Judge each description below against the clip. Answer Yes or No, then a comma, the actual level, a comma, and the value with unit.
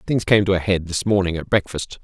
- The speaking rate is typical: No, fast, 265 wpm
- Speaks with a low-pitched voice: Yes, very low, 95 Hz